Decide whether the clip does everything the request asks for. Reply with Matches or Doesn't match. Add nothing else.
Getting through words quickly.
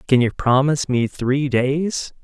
Doesn't match